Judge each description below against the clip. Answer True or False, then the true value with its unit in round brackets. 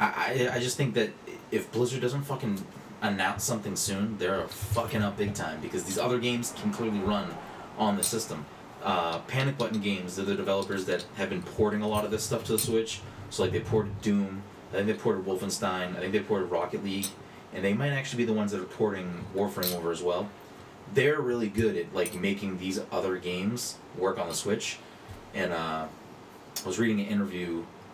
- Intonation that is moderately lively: True (3.0 semitones)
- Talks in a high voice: False (105 Hz)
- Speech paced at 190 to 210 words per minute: True (205 wpm)